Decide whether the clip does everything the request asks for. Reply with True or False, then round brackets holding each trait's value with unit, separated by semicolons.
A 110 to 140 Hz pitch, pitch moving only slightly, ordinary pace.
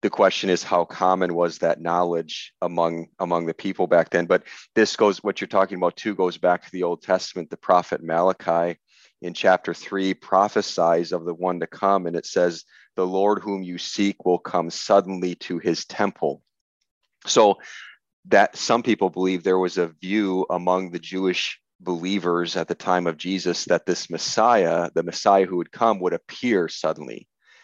False (90 Hz; 1.5 semitones; 180 wpm)